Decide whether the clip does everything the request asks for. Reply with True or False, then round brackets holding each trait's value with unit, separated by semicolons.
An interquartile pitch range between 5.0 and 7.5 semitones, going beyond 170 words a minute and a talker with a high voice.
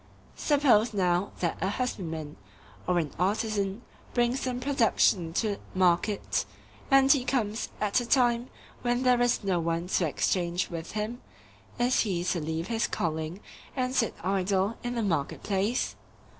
False (5.5 semitones; 145 wpm; 205 Hz)